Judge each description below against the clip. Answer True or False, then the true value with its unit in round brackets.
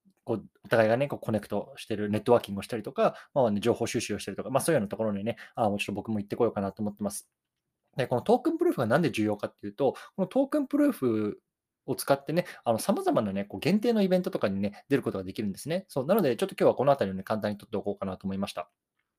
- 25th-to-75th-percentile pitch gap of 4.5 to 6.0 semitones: False (7.9 semitones)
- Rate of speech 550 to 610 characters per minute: True (565 characters per minute)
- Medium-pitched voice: False (110 Hz)